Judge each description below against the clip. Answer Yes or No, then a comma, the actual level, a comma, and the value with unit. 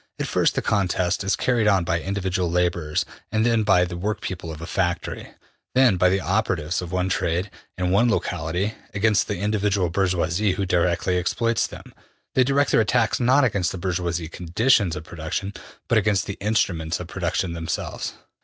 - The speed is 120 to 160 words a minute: No, average, 170 wpm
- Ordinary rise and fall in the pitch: Yes, average, 3.4 semitones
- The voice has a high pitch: No, very low, 95 Hz